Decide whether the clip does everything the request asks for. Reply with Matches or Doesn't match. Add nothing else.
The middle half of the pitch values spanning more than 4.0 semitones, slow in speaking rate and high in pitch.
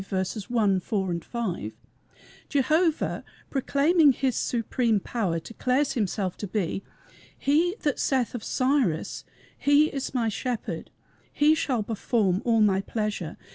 Matches